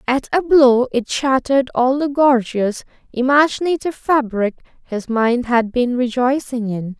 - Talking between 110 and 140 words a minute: Yes, slow, 135 wpm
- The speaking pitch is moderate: No, very high, 255 Hz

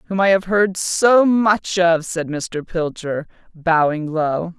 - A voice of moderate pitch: Yes, medium, 175 Hz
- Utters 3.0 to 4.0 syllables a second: Yes, 3.4 syllables/s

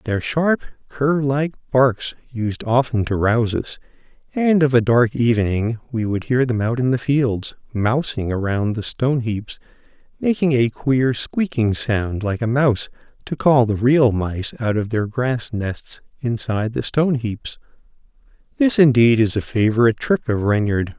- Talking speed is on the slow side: No, average, 165 wpm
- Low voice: Yes, low, 120 Hz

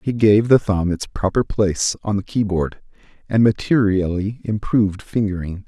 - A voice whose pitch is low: Yes, low, 100 Hz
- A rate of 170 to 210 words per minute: No, average, 150 wpm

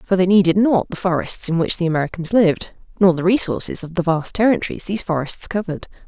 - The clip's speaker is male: No, female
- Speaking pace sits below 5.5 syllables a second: No, 6.5 syllables/s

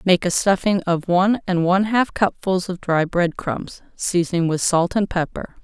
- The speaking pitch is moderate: Yes, medium, 180 Hz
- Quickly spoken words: No, average, 190 wpm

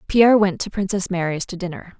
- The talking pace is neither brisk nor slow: No, fast, 210 wpm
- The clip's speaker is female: Yes, female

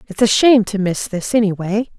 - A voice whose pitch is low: No, high, 205 Hz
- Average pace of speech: No, fast, 210 wpm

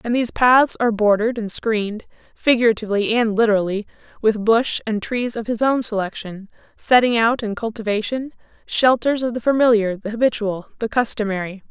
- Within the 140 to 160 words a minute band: Yes, average, 150 wpm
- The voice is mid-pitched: No, high, 225 Hz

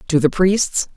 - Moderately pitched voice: Yes, medium, 175 Hz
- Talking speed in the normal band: Yes, average, 190 wpm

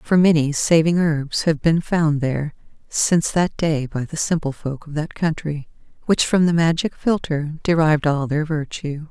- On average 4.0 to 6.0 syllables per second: Yes, 4.6 syllables/s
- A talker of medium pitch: Yes, medium, 155 Hz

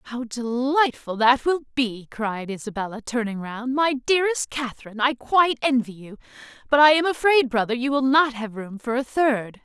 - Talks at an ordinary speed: Yes, average, 180 wpm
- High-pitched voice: Yes, very high, 250 Hz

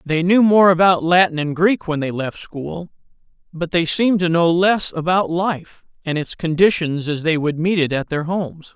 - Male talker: Yes, male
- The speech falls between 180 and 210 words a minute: Yes, fast, 205 wpm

